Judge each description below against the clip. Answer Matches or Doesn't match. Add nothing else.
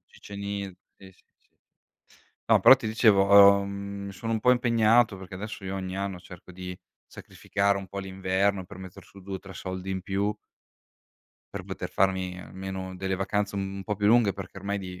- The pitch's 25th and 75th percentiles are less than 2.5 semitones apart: Matches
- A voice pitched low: Matches